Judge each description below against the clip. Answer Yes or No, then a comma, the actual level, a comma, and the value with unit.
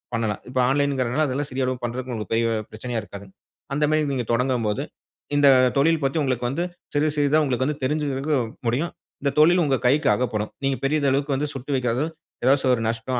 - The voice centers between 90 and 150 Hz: Yes, low, 135 Hz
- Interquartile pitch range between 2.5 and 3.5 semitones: Yes, average, 3.0 semitones